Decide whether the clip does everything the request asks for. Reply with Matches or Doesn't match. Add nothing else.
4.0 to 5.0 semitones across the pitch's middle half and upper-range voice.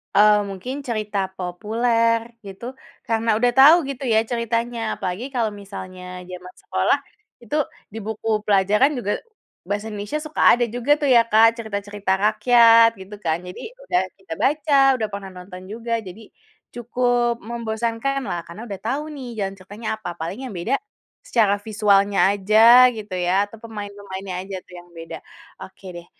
Doesn't match